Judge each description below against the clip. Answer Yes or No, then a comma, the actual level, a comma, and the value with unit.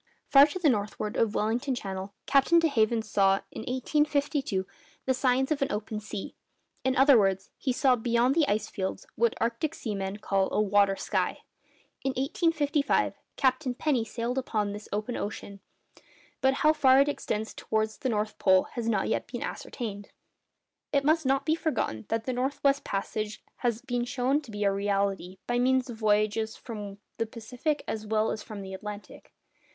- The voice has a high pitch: Yes, high, 230 Hz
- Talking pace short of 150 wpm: No, average, 175 wpm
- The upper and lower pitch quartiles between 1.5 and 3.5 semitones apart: No, average, 4.4 semitones